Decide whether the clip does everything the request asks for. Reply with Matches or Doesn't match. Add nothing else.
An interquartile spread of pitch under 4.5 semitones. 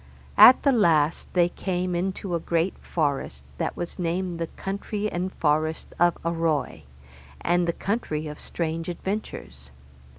Matches